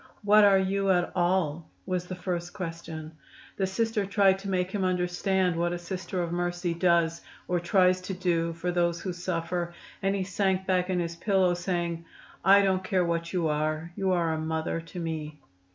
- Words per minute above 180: Yes, average, 190 wpm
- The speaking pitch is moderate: Yes, medium, 180 Hz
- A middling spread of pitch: No, narrow, 2.0 semitones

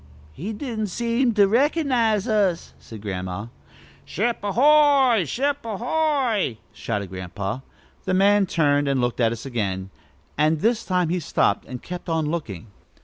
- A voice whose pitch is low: No, medium, 185 Hz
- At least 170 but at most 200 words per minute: No, average, 150 wpm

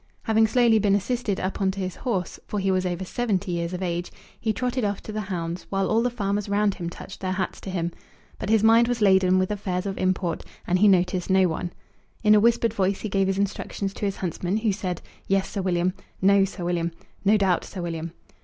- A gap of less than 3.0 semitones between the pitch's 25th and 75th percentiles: Yes, narrow, 2.4 semitones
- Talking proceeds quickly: Yes, fast, 230 wpm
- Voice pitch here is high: Yes, high, 195 Hz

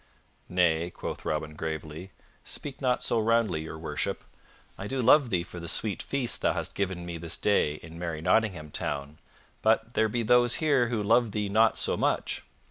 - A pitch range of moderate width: No, wide, 6.1 semitones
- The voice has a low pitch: Yes, low, 100 Hz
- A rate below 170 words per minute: No, average, 185 wpm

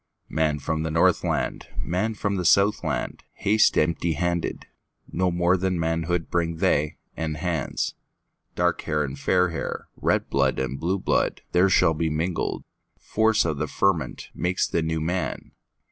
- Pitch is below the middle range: Yes, very low, 85 Hz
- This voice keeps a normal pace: No, slow, 120 wpm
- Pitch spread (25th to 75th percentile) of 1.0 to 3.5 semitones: Yes, narrow, 2.5 semitones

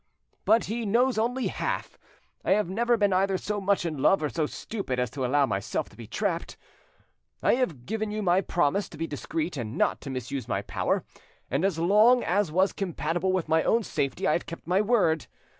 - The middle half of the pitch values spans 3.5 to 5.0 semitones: No, wide, 5.6 semitones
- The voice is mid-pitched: Yes, medium, 180 Hz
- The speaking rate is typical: No, fast, 210 wpm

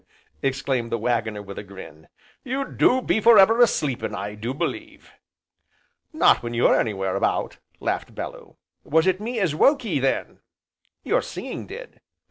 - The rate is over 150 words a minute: Yes, average, 160 wpm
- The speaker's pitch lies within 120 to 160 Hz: Yes, low, 135 Hz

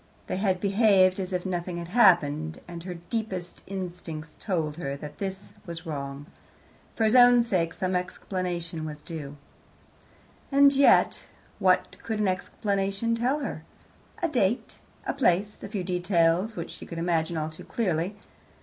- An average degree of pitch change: Yes, average, 3.6 semitones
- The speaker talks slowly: No, average, 155 wpm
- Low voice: No, medium, 180 Hz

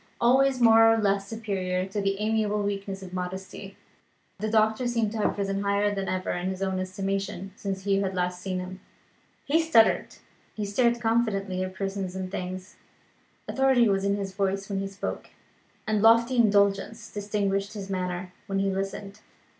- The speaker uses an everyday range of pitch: No, narrow, 2.2 semitones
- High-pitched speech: Yes, high, 200 Hz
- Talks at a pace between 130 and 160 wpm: No, average, 170 wpm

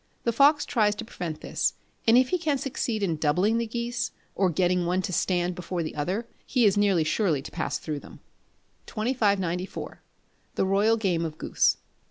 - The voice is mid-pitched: No, high, 195 Hz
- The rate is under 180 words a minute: No, average, 185 wpm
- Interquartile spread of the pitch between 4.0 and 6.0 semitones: Yes, average, 4.7 semitones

